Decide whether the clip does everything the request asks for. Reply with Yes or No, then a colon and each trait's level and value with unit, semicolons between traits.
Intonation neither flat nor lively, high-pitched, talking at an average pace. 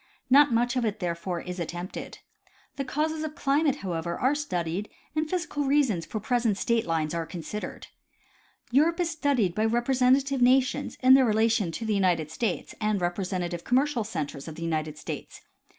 No: wide, 7.5 semitones; high, 220 Hz; average, 170 wpm